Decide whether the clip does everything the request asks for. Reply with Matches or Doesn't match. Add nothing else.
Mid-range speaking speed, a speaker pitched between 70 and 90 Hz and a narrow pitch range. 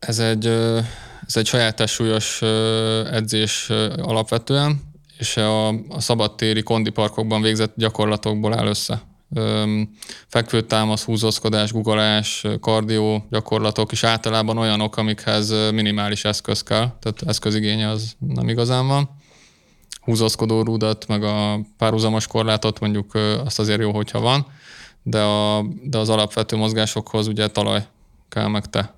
Doesn't match